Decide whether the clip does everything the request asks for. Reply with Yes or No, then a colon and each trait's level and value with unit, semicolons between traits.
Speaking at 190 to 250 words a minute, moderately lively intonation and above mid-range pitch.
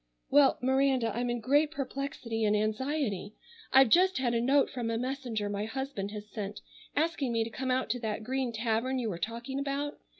Yes: average, 195 wpm; average, 3.7 semitones; high, 245 Hz